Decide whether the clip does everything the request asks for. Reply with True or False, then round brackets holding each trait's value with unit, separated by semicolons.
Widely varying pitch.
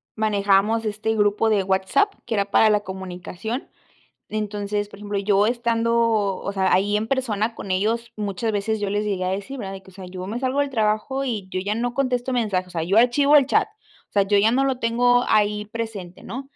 False (2.9 semitones)